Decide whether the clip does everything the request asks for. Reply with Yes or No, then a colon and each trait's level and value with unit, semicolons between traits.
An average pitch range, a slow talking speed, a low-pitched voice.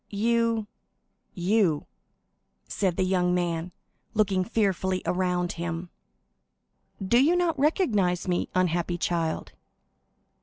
No: average, 3.8 semitones; slow, 90 wpm; medium, 185 Hz